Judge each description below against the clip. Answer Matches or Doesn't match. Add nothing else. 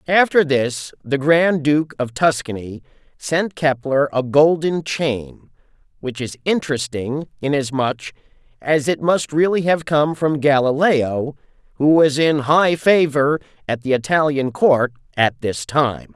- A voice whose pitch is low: Doesn't match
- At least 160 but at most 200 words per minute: Doesn't match